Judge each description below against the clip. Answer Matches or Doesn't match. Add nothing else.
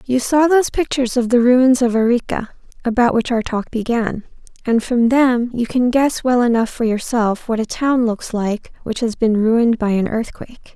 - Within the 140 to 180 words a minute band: Doesn't match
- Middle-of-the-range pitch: Doesn't match